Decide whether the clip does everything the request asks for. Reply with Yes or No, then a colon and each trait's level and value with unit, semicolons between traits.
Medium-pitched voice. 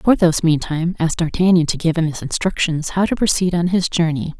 Yes: medium, 170 Hz